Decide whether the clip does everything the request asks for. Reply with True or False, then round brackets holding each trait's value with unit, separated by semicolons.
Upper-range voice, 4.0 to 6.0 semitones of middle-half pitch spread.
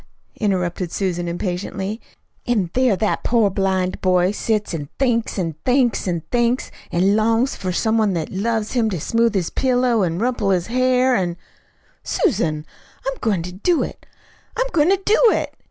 True (210 Hz; 5.0 semitones)